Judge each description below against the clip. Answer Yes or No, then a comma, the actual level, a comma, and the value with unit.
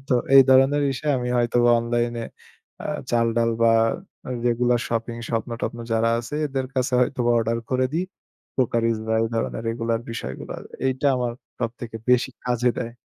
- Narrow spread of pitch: Yes, narrow, 1.6 semitones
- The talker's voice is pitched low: Yes, low, 120 Hz